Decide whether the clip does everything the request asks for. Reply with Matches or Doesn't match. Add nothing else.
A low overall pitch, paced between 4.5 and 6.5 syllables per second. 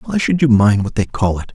Matches